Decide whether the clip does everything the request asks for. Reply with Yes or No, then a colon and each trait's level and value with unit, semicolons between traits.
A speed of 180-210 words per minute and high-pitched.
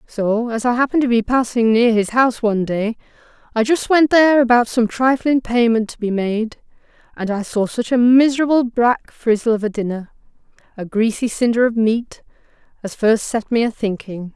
Yes: average, 185 wpm; high, 230 Hz